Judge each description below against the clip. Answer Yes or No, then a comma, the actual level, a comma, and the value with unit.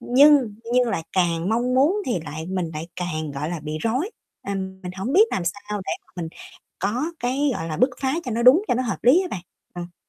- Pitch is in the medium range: No, high, 200 Hz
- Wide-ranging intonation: Yes, wide, 6.7 semitones